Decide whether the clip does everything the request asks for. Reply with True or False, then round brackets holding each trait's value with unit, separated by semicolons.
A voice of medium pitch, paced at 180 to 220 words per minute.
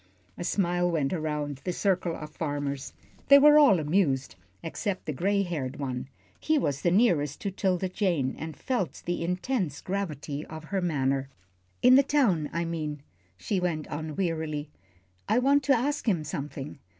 False (170 Hz; 160 wpm)